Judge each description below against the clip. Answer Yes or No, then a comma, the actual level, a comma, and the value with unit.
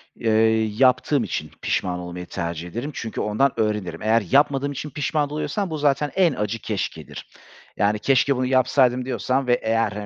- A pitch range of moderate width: Yes, average, 4.7 semitones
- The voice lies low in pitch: Yes, low, 125 Hz